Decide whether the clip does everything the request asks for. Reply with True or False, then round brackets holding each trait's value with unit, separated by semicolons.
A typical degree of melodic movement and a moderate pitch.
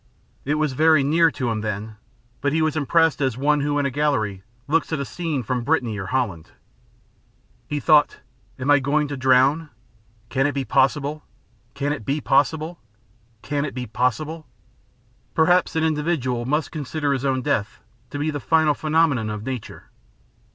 True (3.2 semitones; 145 Hz)